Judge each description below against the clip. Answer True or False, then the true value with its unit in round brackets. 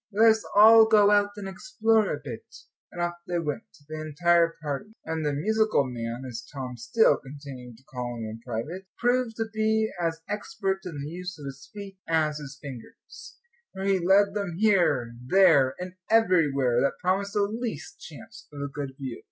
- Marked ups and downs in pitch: True (6.8 semitones)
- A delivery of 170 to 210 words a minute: True (185 wpm)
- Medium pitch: True (170 Hz)